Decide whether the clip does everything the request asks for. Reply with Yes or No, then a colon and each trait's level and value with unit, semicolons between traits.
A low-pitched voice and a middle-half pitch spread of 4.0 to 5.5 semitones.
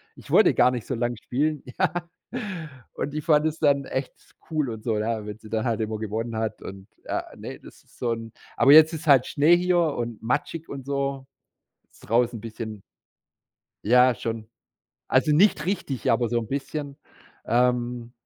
Yes: low, 125 Hz; average, 4.4 semitones